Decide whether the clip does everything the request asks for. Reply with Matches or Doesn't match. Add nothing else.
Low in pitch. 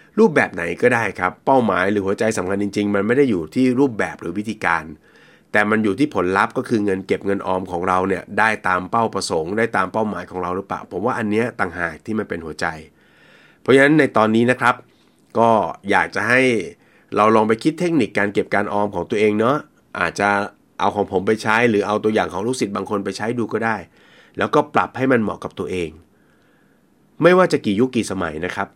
Matches